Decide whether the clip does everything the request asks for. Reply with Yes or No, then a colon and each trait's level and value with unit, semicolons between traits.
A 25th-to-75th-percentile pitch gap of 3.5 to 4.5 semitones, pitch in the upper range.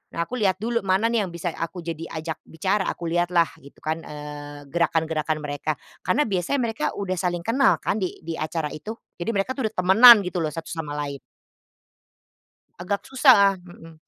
No: average, 4.0 semitones; medium, 175 Hz